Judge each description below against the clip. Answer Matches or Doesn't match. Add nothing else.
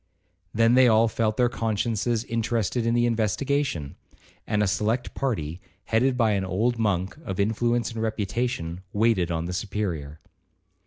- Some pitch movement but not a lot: Matches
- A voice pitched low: Matches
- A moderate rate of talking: Matches